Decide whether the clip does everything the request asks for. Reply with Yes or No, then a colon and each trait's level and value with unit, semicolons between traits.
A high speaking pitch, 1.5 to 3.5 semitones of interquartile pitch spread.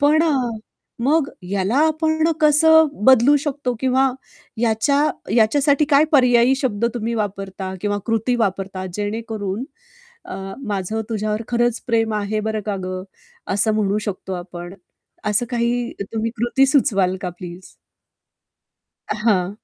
No: high, 225 Hz; average, 4.4 semitones